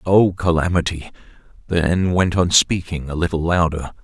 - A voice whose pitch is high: No, very low, 85 Hz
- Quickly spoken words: No, slow, 135 wpm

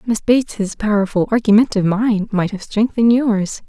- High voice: Yes, high, 215 Hz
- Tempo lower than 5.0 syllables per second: No, 5.4 syllables/s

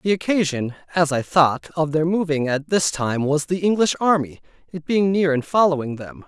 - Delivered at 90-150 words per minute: No, average, 200 wpm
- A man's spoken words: Yes, male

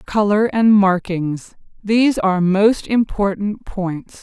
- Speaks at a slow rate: Yes, slow, 100 wpm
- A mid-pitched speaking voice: No, high, 200 Hz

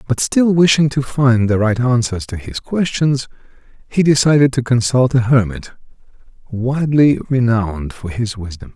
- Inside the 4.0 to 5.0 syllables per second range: Yes, 4.8 syllables/s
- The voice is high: No, low, 125 Hz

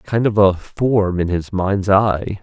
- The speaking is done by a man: Yes, male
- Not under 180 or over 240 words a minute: Yes, average, 200 wpm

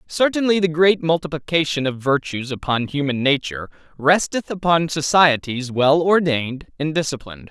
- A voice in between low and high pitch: Yes, medium, 155 Hz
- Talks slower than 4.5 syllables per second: No, 5.1 syllables/s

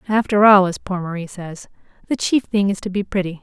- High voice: Yes, high, 195 Hz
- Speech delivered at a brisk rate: Yes, fast, 230 wpm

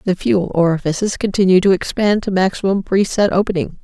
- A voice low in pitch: No, medium, 185 Hz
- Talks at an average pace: Yes, average, 170 wpm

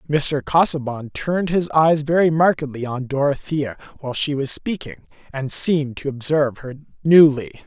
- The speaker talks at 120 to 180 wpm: Yes, average, 150 wpm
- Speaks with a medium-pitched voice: Yes, medium, 145 Hz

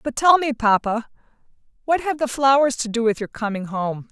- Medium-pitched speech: No, high, 245 Hz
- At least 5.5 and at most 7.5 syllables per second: No, 5.2 syllables/s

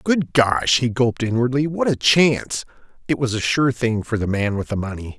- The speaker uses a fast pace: Yes, fast, 220 wpm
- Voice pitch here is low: Yes, low, 120 Hz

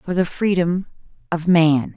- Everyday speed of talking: Yes, average, 155 wpm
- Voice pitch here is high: No, medium, 170 Hz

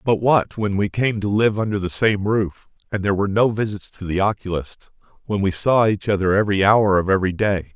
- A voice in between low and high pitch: No, low, 100 Hz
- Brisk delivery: Yes, fast, 225 wpm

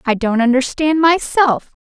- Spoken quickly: No, slow, 130 wpm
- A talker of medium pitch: No, very high, 275 Hz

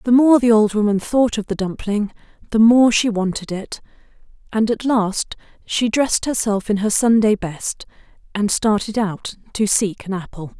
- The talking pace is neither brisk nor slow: Yes, average, 175 wpm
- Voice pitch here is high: Yes, high, 215 Hz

